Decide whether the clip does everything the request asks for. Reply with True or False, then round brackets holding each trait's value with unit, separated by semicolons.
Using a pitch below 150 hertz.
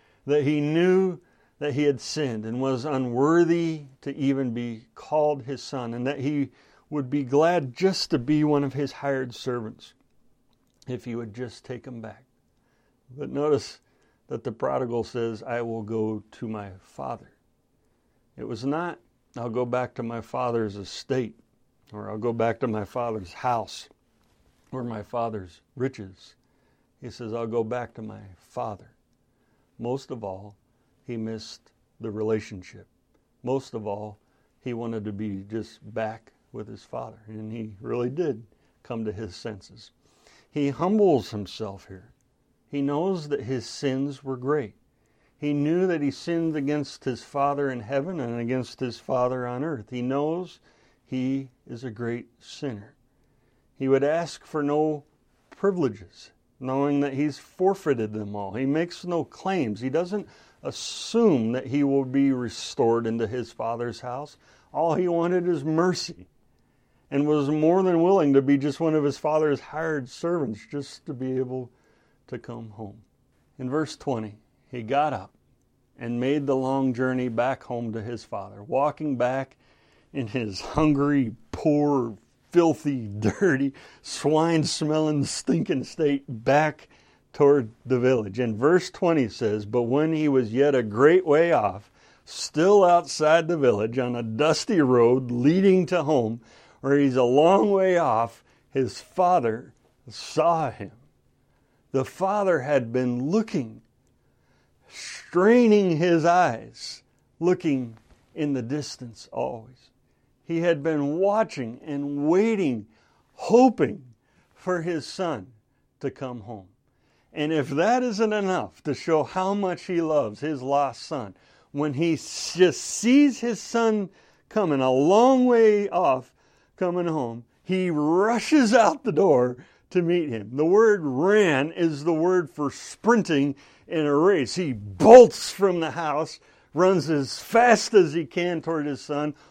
True (135 Hz)